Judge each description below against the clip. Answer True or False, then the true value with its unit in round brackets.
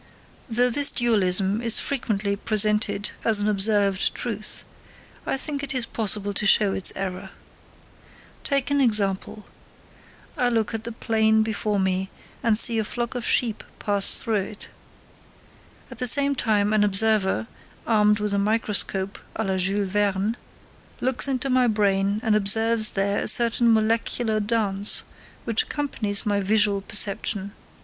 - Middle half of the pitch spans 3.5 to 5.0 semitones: False (2.4 semitones)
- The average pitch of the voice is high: True (215 Hz)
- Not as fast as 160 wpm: True (145 wpm)